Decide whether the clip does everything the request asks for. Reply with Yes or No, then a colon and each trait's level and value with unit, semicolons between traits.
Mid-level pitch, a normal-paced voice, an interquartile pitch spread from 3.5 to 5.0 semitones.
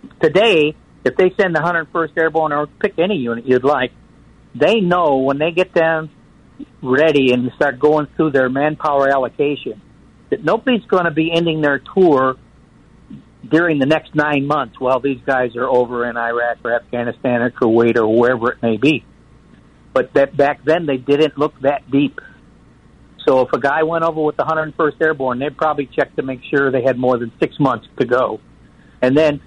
Yes: medium, 145 Hz; average, 185 wpm; average, 3.8 semitones